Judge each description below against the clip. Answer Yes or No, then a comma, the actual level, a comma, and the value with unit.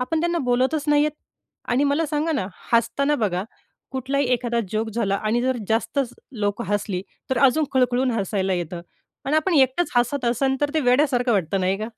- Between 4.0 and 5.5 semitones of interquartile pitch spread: Yes, average, 4.5 semitones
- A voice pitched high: Yes, very high, 250 Hz